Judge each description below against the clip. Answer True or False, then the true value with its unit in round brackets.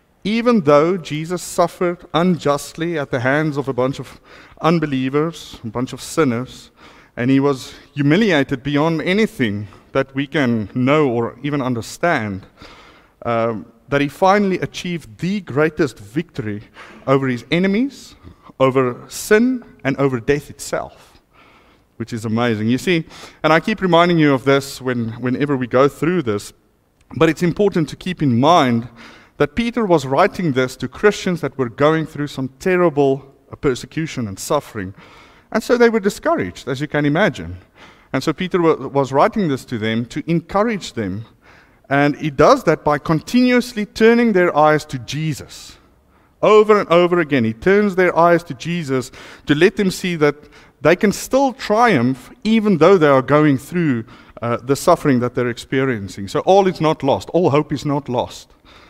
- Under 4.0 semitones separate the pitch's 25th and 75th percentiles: False (5.4 semitones)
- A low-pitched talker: False (145 Hz)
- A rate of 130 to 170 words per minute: True (165 wpm)